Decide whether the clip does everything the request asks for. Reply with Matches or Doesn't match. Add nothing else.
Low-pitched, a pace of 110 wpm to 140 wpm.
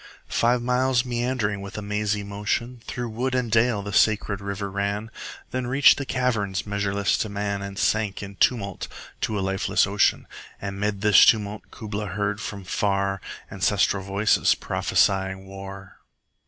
Doesn't match